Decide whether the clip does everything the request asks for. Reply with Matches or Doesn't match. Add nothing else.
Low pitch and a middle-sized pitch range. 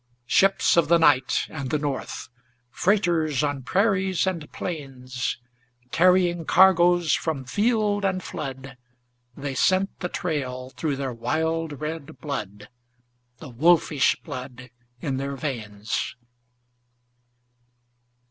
Doesn't match